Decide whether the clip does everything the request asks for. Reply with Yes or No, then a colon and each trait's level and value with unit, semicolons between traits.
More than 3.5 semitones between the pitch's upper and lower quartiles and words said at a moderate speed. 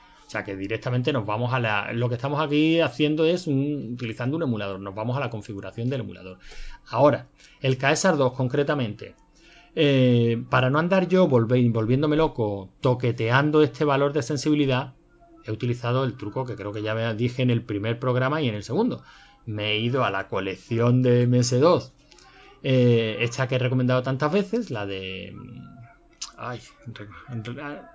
Yes: average, 4.1 semitones; average, 170 wpm